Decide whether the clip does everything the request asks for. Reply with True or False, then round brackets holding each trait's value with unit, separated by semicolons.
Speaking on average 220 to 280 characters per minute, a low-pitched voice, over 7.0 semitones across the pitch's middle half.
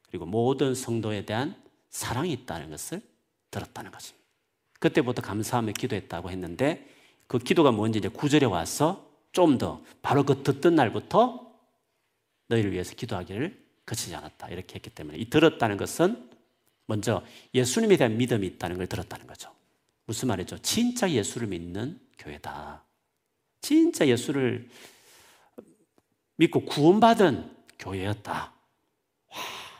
False (295 characters per minute; 120 Hz; 7.4 semitones)